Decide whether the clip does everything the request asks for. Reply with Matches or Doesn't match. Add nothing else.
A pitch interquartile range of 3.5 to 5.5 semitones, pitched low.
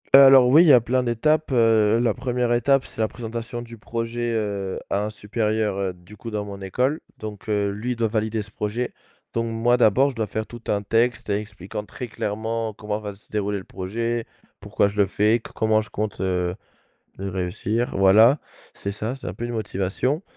Doesn't match